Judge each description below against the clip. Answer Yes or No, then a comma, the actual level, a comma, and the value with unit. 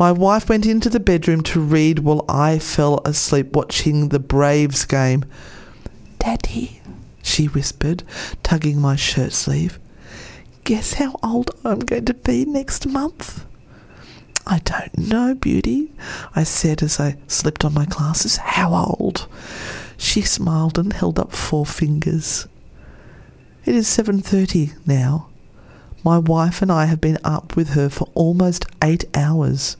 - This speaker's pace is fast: No, average, 140 wpm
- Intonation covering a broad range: No, average, 3.8 semitones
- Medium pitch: Yes, medium, 155 Hz